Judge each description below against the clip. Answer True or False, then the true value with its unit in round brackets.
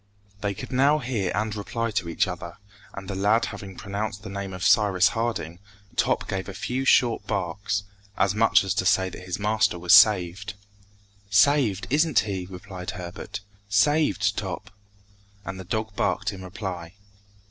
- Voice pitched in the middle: False (100 Hz)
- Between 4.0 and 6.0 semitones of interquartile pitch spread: False (2.6 semitones)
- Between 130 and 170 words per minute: True (165 wpm)